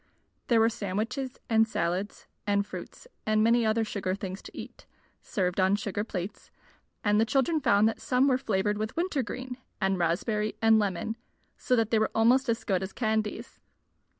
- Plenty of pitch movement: No, narrow, 2.6 semitones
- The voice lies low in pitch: No, high, 215 Hz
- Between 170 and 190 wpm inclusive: Yes, average, 180 wpm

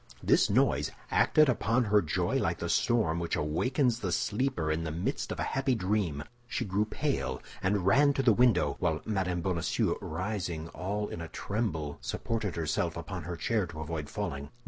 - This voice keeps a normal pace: Yes, average, 180 wpm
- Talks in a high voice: No, very low, 95 Hz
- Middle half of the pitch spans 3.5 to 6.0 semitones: Yes, wide, 5.6 semitones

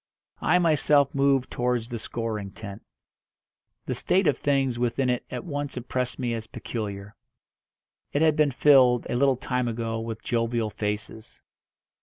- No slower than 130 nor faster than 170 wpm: Yes, average, 150 wpm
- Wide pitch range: No, average, 3.4 semitones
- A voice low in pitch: Yes, low, 125 Hz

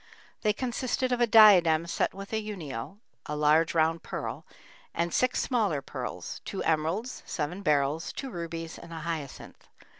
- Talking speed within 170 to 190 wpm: No, average, 155 wpm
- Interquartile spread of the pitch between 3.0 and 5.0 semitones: No, wide, 5.4 semitones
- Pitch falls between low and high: Yes, medium, 170 Hz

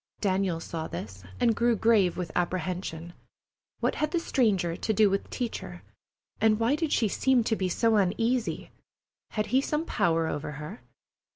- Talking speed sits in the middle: Yes, average, 170 wpm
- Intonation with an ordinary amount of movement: Yes, average, 4.9 semitones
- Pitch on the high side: Yes, high, 200 Hz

